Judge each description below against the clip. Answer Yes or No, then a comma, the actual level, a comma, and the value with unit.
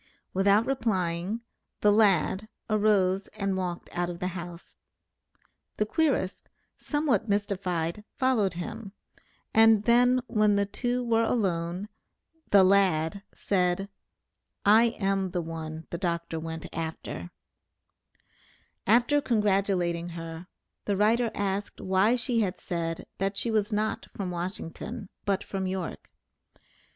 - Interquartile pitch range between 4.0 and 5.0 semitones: No, average, 3.6 semitones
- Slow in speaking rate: Yes, slow, 120 wpm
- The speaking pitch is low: No, high, 195 Hz